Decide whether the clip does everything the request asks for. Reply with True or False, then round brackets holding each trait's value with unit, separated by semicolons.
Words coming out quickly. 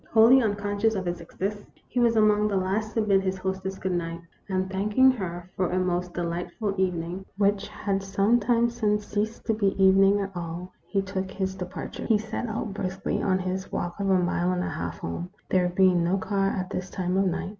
True (210 wpm)